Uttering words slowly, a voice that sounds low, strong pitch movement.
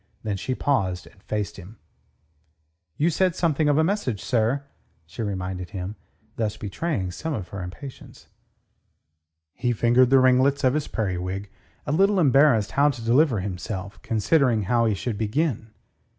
No: average, 150 wpm; low, 115 Hz; wide, 6.1 semitones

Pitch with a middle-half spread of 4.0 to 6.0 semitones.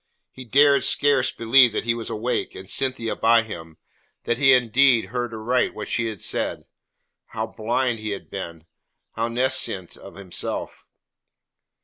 No: average, 2.9 semitones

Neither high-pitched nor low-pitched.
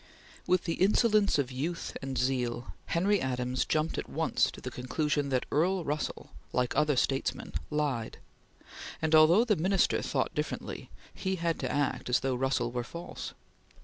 Yes: medium, 150 Hz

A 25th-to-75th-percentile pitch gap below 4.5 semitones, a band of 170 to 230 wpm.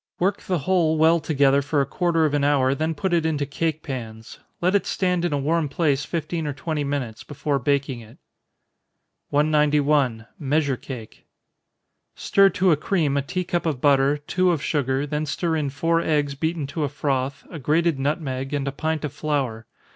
Yes: average, 2.8 semitones; average, 190 wpm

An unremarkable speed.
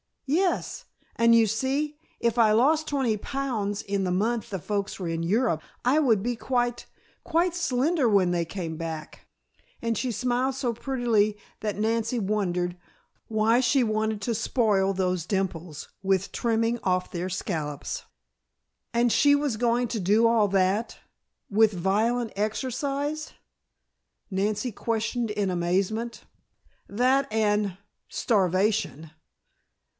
No: slow, 130 wpm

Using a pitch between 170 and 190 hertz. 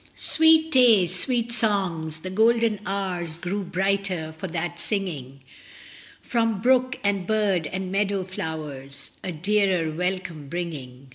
Yes: medium, 185 Hz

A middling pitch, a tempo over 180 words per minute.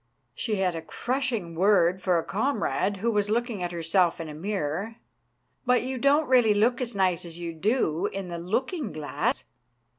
No: high, 200 Hz; average, 190 wpm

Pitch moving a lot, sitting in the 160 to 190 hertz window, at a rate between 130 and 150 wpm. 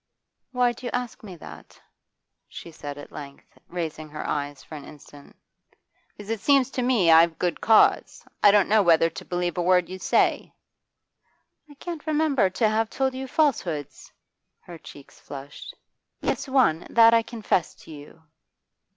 No: wide, 7.5 semitones; medium, 185 Hz; average, 165 wpm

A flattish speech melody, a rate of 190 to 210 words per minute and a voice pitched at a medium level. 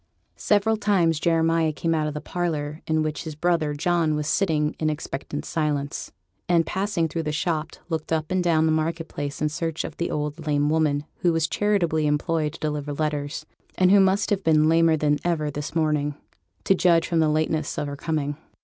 Yes: narrow, 1.9 semitones; average, 200 wpm; medium, 155 Hz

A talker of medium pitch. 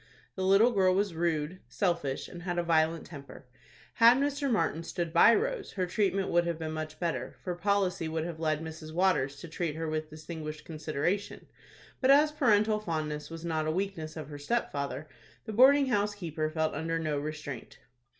Yes: medium, 170 Hz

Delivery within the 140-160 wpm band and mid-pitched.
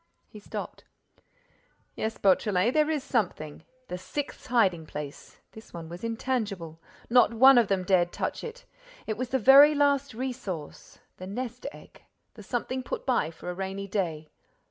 No: average, 155 wpm; high, 220 Hz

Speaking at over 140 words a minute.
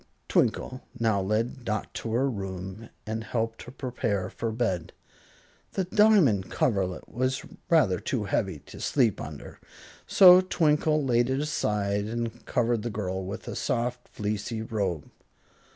No: slow, 135 wpm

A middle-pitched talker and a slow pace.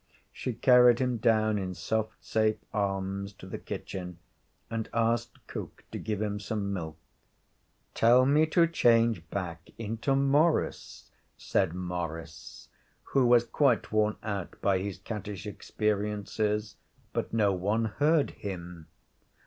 No: low, 105 Hz; slow, 130 wpm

